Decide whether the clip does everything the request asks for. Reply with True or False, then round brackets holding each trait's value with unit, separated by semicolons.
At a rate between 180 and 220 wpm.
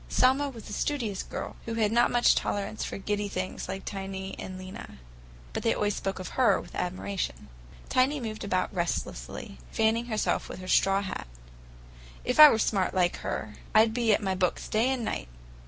True (190 wpm)